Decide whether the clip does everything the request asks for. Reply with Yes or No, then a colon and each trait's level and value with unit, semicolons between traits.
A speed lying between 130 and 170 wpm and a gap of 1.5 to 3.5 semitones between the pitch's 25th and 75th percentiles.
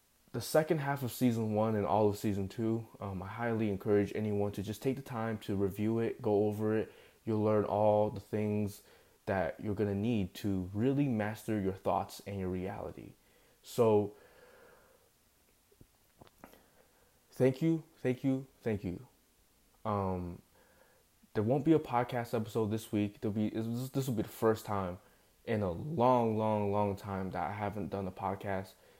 Yes: average, 165 wpm; average, 3.0 semitones